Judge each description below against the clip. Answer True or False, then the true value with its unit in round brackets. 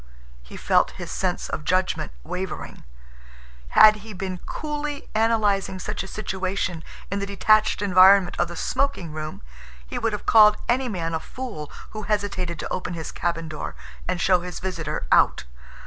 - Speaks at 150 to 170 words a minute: True (165 wpm)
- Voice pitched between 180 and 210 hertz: True (190 Hz)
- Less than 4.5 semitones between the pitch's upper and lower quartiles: True (3.7 semitones)